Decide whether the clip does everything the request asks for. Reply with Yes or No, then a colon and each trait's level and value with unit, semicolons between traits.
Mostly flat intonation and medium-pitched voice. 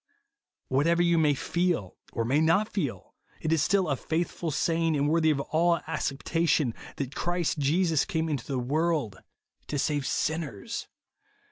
No: average, 3.4 semitones; medium, 160 Hz